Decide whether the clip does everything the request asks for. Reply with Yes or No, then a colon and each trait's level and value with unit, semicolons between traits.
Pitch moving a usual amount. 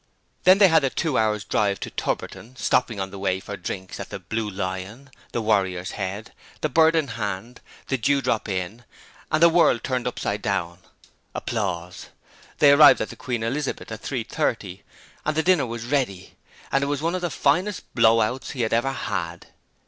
No: wide, 6.3 semitones